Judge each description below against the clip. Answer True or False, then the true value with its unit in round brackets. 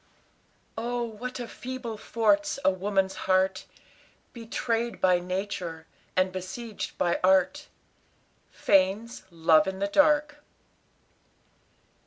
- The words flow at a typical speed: False (100 wpm)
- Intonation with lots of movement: False (4.2 semitones)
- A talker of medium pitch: False (205 Hz)